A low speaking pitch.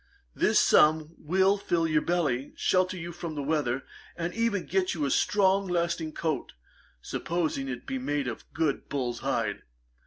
No: medium, 160 Hz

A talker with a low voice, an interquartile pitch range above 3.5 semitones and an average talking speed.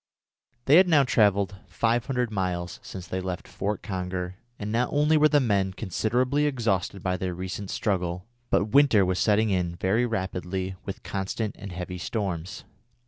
Yes: low, 100 Hz; average, 4.1 semitones; average, 160 wpm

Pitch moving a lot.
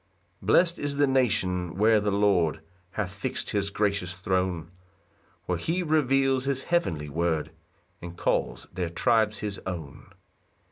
Yes: wide, 6.7 semitones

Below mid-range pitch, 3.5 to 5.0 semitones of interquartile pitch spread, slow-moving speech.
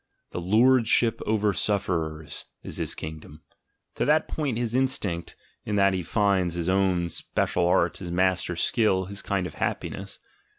No: very low, 95 Hz; average, 3.8 semitones; average, 160 wpm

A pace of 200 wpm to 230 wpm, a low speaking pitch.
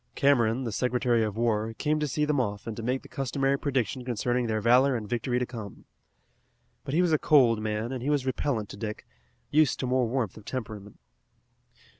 Yes: fast, 205 wpm; low, 125 Hz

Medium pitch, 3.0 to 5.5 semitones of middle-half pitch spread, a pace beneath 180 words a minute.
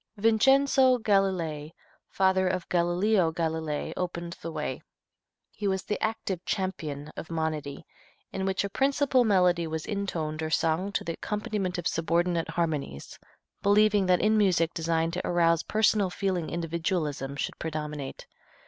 Yes: medium, 175 Hz; average, 3.8 semitones; average, 140 wpm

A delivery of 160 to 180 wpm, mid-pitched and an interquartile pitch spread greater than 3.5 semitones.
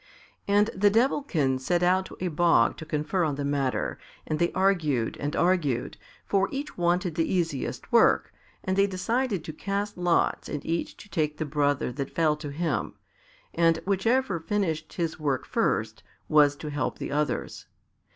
Yes: average, 170 wpm; medium, 165 Hz; average, 4.4 semitones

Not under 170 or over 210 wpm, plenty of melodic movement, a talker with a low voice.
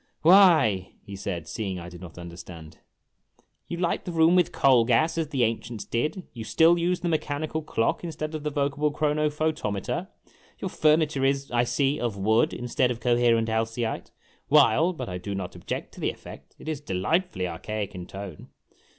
Yes: average, 180 wpm; wide, 7.4 semitones; low, 125 Hz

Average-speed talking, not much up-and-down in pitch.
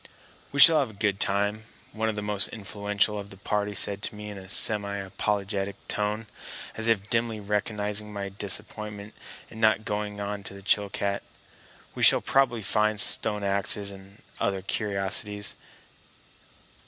Yes: average, 155 wpm; narrow, 1.1 semitones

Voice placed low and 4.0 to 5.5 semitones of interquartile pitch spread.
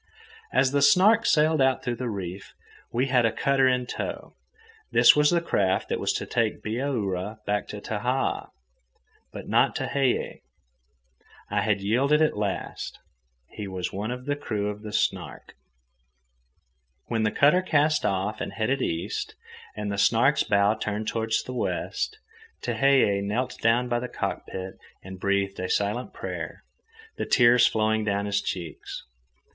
Yes: low, 110 Hz; average, 4.7 semitones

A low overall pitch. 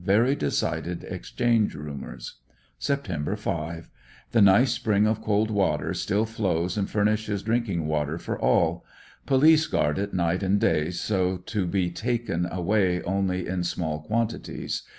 Yes: very low, 95 Hz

